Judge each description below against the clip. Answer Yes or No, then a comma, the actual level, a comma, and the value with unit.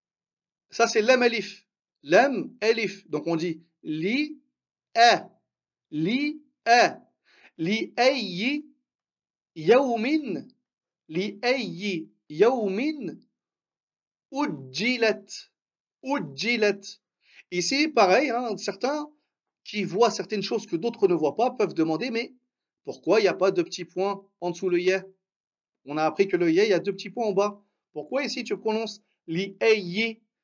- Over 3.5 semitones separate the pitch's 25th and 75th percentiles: Yes, average, 4.9 semitones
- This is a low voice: No, high, 215 Hz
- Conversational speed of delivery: No, slow, 130 wpm